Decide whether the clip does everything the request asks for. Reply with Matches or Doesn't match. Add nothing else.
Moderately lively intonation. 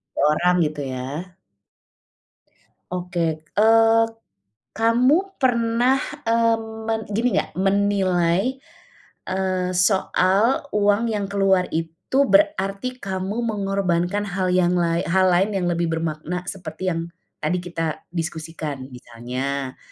Matches